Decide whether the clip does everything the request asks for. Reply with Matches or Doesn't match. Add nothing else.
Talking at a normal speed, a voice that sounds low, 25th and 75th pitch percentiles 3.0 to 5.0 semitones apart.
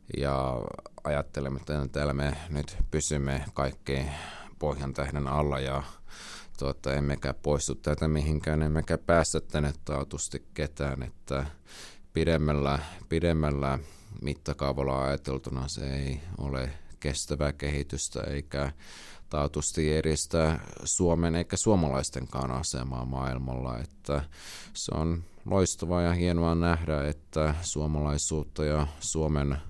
Doesn't match